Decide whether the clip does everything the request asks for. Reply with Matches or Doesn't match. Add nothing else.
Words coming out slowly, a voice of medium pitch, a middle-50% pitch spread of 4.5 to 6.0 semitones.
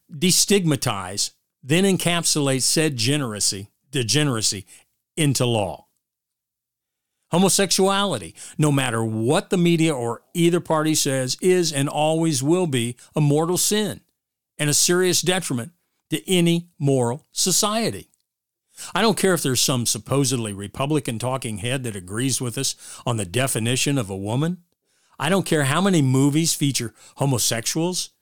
Matches